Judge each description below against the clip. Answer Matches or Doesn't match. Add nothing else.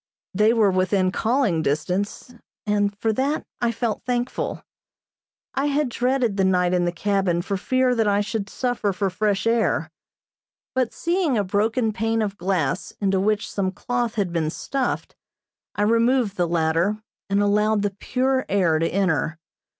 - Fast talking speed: Doesn't match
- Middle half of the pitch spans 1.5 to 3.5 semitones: Doesn't match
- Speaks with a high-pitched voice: Matches